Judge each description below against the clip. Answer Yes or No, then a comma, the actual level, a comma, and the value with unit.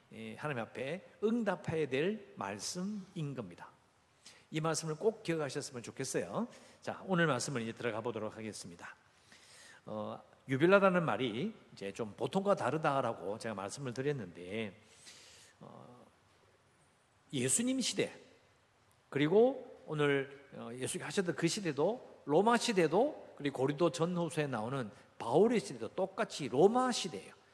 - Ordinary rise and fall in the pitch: No, wide, 8.0 semitones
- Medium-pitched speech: Yes, medium, 150 Hz